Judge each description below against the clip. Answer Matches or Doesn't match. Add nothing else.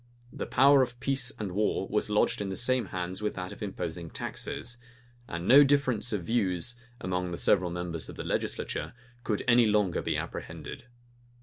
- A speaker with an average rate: Matches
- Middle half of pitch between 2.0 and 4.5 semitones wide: Doesn't match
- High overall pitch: Doesn't match